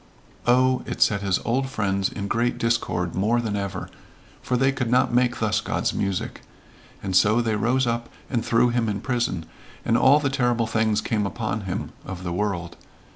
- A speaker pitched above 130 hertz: No, low, 115 Hz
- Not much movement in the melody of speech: No, average, 3.5 semitones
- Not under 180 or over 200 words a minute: Yes, average, 185 wpm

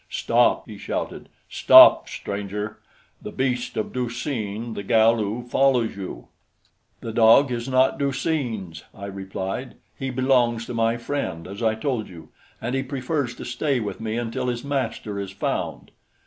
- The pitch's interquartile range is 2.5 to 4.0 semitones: Yes, average, 3.7 semitones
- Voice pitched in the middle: No, low, 115 Hz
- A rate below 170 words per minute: Yes, average, 160 wpm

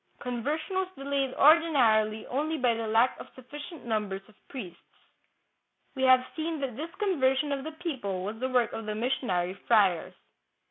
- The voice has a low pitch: No, very high, 255 Hz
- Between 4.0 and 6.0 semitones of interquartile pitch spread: Yes, average, 5.2 semitones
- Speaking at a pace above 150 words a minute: Yes, average, 165 wpm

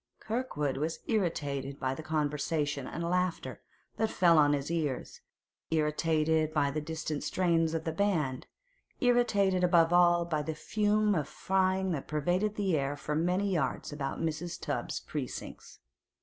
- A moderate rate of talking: Yes, average, 150 wpm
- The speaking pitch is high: No, medium, 160 Hz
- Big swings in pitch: No, average, 3.5 semitones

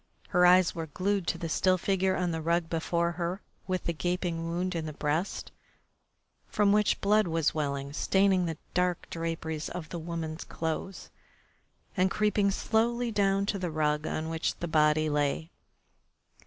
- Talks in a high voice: No, medium, 170 Hz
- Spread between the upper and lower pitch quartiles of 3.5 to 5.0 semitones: No, average, 2.9 semitones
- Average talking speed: Yes, average, 170 wpm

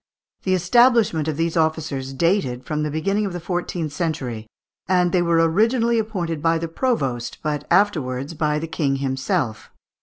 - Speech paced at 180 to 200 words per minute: No, average, 160 wpm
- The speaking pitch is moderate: Yes, medium, 165 Hz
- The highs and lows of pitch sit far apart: No, average, 4.2 semitones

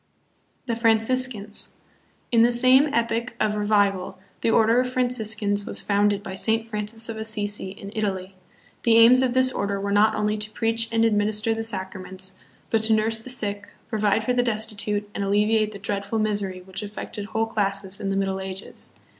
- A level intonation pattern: Yes, narrow, 2.0 semitones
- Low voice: No, high, 215 Hz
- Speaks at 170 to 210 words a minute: Yes, average, 180 wpm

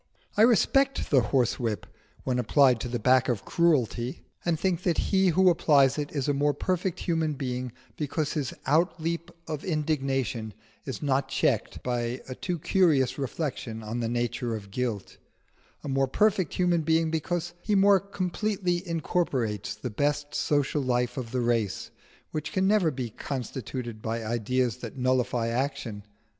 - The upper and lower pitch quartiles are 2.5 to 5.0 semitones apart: No, wide, 5.4 semitones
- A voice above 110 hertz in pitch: Yes, low, 135 Hz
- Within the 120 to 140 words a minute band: No, average, 155 wpm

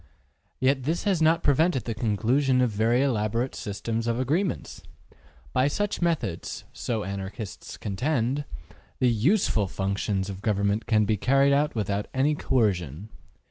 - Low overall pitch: Yes, low, 120 Hz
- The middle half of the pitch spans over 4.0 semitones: Yes, average, 5.2 semitones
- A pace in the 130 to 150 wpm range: Yes, average, 140 wpm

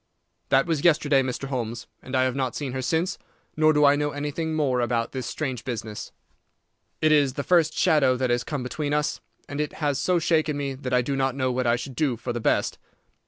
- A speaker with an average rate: No, fast, 225 wpm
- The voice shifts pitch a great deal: No, average, 2.9 semitones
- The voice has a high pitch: No, low, 135 Hz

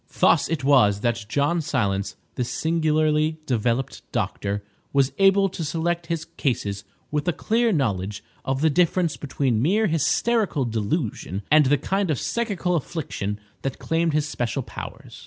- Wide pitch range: Yes, wide, 5.9 semitones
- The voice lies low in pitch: No, medium, 150 Hz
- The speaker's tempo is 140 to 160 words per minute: Yes, average, 150 wpm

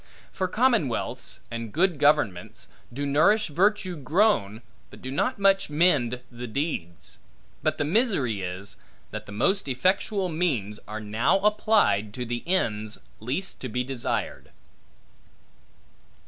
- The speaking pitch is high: No, medium, 140 Hz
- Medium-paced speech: No, slow, 130 wpm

